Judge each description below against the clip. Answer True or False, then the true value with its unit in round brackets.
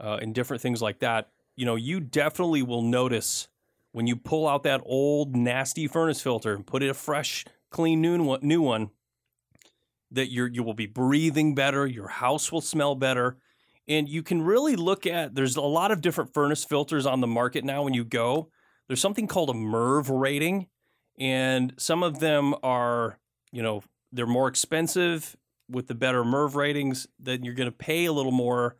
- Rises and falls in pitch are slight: False (3.8 semitones)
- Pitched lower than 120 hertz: False (135 Hz)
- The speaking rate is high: False (190 wpm)